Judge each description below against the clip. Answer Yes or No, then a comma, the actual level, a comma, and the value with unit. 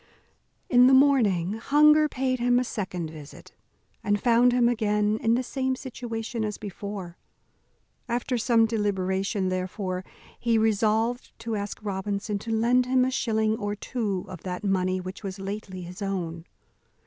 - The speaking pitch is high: Yes, high, 215 Hz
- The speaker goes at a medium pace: Yes, average, 150 wpm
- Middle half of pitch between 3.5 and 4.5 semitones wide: Yes, average, 4.1 semitones